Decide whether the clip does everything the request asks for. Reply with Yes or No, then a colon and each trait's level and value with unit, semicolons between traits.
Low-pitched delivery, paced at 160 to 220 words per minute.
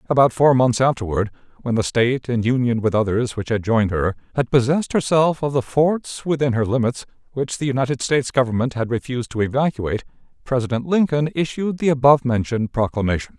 Yes: low, 125 Hz; average, 180 wpm